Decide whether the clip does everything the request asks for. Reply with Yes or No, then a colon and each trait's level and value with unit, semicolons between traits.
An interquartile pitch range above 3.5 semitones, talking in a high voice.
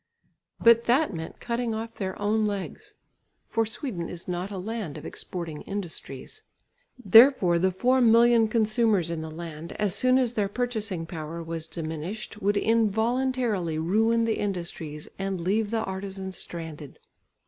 Yes: average, 5.0 semitones; high, 200 Hz